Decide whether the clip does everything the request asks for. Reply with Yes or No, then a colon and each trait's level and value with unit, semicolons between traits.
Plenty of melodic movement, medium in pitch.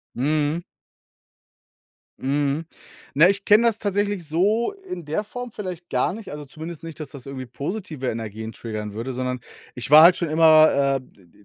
Yes: wide, 5.9 semitones; medium, 155 Hz